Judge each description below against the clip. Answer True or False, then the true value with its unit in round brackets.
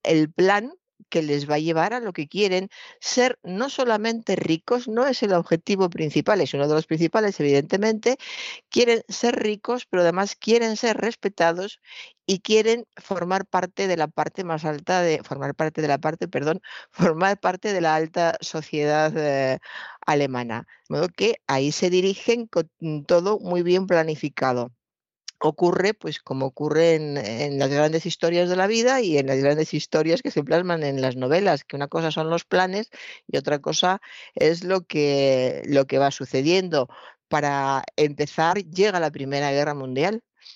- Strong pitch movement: False (5.0 semitones)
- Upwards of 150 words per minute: True (170 wpm)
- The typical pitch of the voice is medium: True (170 Hz)